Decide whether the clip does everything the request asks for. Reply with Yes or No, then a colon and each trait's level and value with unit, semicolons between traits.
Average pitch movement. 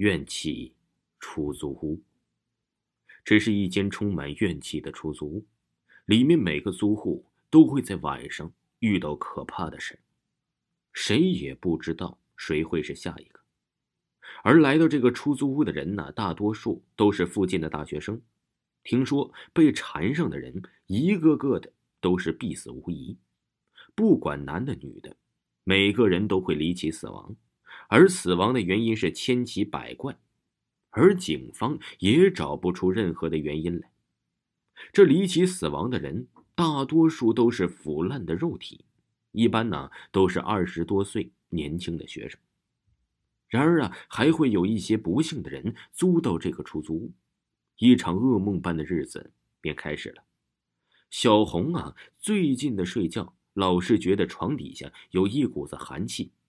No: wide, 6.5 semitones